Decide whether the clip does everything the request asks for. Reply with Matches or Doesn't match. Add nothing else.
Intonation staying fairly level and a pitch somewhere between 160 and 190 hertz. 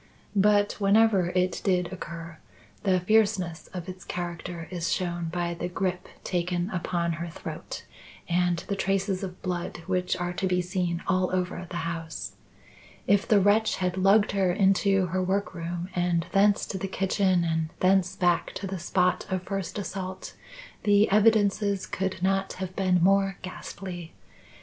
Matches